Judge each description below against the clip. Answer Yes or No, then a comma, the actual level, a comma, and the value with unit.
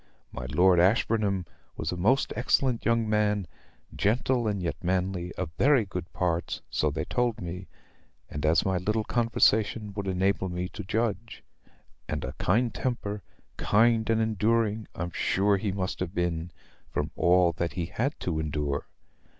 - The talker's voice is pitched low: Yes, very low, 95 Hz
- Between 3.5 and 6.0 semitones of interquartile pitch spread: Yes, average, 4.1 semitones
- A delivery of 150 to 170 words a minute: Yes, average, 160 wpm